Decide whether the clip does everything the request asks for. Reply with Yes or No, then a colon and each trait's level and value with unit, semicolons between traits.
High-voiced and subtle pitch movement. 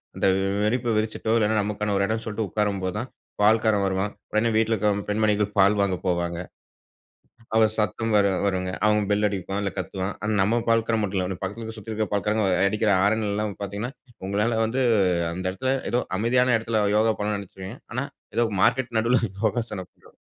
No: low, 105 Hz; narrow, 2.1 semitones